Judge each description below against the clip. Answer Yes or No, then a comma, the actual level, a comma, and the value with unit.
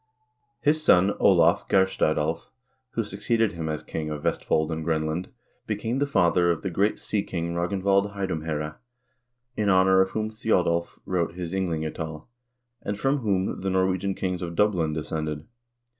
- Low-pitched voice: Yes, very low, 90 Hz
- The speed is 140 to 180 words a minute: Yes, average, 155 wpm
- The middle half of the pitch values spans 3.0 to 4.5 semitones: Yes, average, 3.6 semitones